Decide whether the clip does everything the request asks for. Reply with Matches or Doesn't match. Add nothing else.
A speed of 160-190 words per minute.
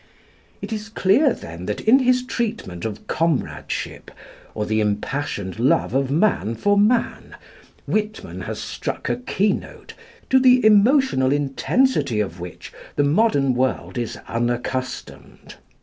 Doesn't match